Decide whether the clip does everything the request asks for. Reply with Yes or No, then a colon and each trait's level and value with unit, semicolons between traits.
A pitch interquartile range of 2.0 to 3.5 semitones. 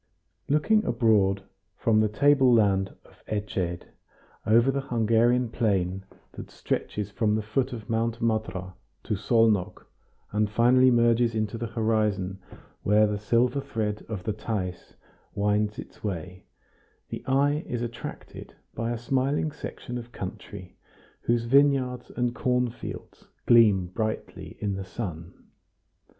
Yes: average, 2.9 semitones